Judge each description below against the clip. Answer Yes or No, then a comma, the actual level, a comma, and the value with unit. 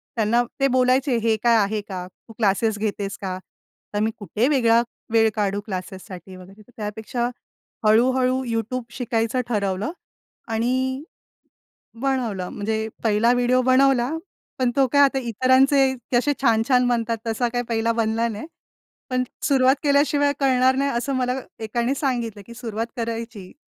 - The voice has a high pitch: Yes, high, 235 Hz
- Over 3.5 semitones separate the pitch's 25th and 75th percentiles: No, average, 2.9 semitones